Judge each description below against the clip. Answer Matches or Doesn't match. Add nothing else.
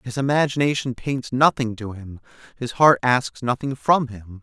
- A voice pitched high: Doesn't match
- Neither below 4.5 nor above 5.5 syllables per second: Matches